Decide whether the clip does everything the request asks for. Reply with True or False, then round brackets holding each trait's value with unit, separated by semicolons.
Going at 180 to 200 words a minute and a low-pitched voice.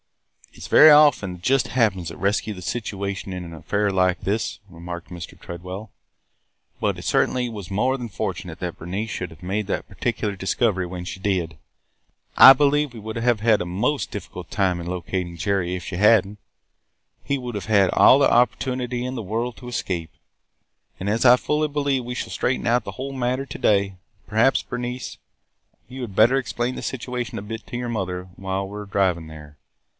True (195 wpm; 105 Hz)